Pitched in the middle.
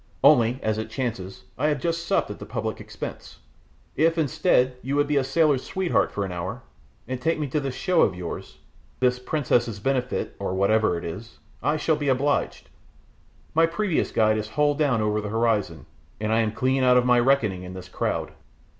No: low, 125 Hz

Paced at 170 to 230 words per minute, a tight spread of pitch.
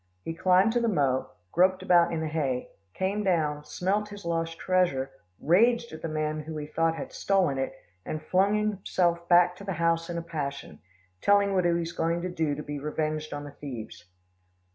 No: average, 200 wpm; average, 3.5 semitones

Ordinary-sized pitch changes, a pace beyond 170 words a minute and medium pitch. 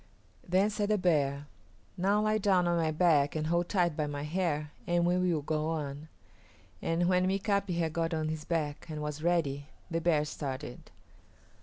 Yes: average, 3.2 semitones; average, 180 wpm; medium, 165 Hz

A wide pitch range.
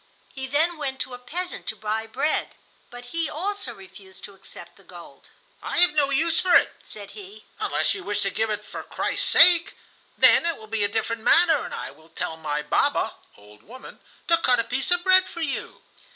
Yes: wide, 8.2 semitones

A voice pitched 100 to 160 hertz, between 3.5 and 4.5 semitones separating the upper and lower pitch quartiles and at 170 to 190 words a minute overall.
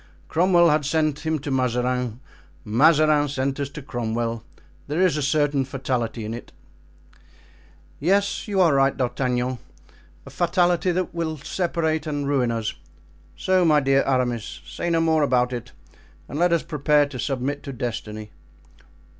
No: medium, 140 Hz; average, 4.1 semitones; average, 150 wpm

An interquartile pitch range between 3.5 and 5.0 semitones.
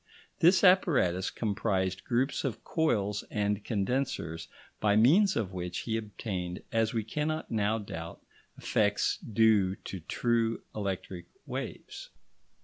Yes: average, 3.9 semitones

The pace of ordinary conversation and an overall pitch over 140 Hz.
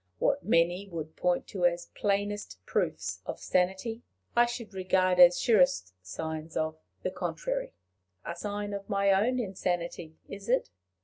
Yes: average, 145 wpm; high, 190 Hz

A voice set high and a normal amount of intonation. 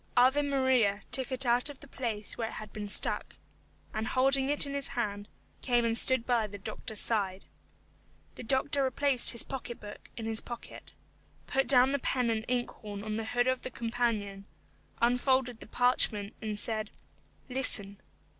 Yes: high, 240 Hz; average, 3.3 semitones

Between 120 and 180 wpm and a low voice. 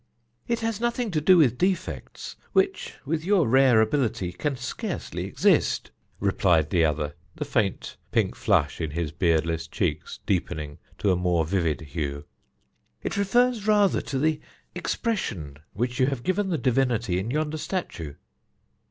Yes: average, 150 wpm; low, 120 Hz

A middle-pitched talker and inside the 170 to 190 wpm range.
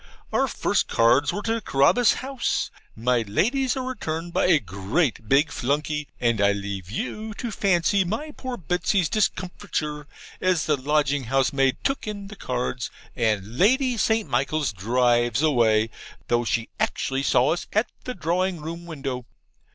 No: medium, 150 Hz; average, 155 wpm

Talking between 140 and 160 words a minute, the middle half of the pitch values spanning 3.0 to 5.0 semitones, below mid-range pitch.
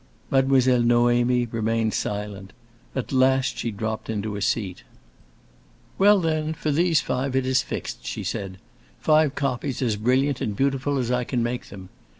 Yes: average, 155 wpm; average, 3.6 semitones; low, 125 Hz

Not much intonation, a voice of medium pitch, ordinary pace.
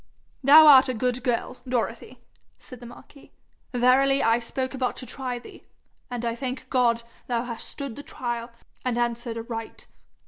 No: narrow, 1.7 semitones; high, 245 Hz; average, 165 wpm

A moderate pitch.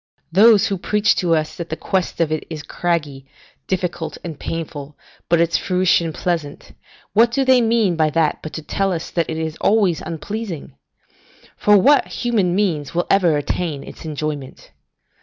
Yes: medium, 170 Hz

